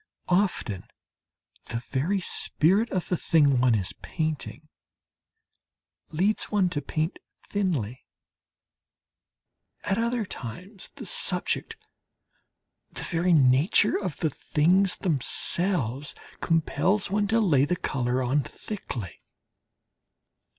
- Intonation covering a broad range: Yes, wide, 6.5 semitones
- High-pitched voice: No, medium, 165 Hz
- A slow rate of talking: Yes, slow, 100 wpm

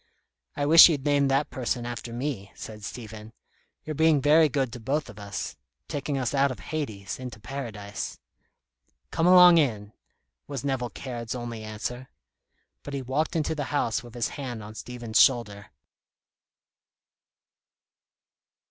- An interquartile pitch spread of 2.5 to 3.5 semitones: No, average, 4.3 semitones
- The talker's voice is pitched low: Yes, low, 125 Hz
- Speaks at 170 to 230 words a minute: No, average, 145 wpm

